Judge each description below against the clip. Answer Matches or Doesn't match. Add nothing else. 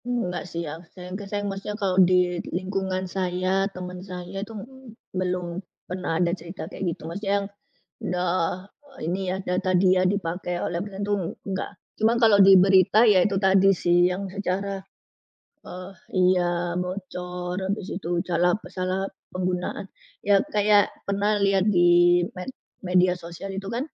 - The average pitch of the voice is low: Doesn't match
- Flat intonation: Matches